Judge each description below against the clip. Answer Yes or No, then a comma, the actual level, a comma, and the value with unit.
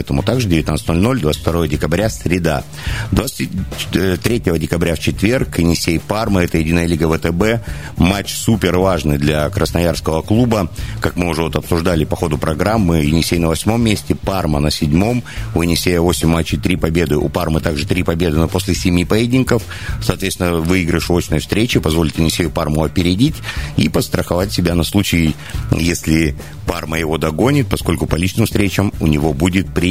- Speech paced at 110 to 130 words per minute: No, average, 155 wpm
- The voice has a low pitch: Yes, very low, 85 Hz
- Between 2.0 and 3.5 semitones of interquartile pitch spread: Yes, average, 3.2 semitones